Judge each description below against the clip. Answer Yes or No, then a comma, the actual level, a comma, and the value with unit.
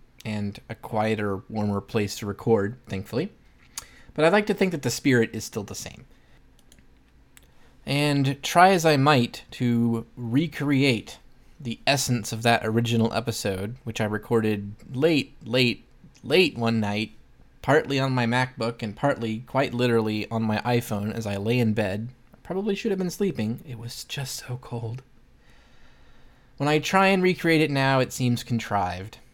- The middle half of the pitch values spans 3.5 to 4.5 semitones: Yes, average, 3.8 semitones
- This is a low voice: Yes, low, 120 Hz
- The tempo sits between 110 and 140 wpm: No, average, 160 wpm